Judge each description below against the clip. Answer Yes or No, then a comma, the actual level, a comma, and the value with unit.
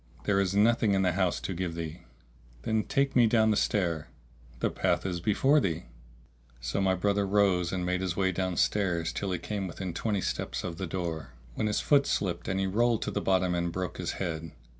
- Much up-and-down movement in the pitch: No, average, 2.9 semitones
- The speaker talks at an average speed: No, fast, 210 wpm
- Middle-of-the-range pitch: No, very low, 95 Hz